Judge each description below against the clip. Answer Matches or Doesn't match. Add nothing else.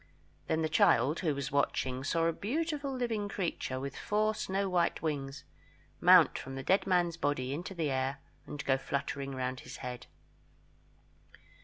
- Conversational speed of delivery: Matches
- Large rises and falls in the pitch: Matches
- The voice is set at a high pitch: Doesn't match